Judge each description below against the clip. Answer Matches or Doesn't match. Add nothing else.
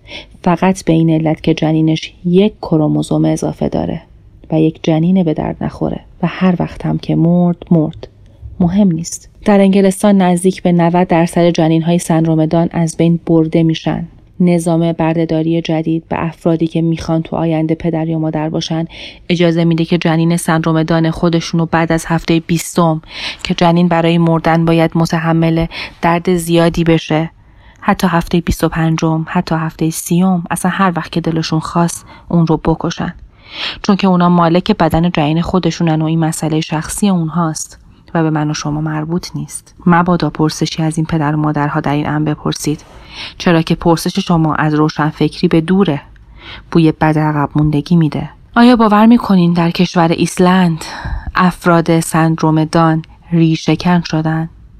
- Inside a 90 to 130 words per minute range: Doesn't match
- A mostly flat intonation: Matches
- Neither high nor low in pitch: Matches